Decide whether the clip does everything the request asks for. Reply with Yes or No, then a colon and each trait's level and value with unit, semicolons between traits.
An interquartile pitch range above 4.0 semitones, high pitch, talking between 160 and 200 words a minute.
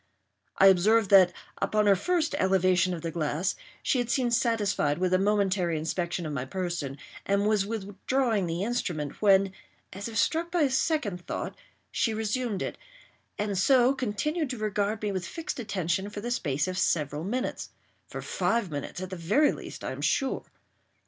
Yes: average, 4.6 semitones; high, 200 Hz; average, 175 wpm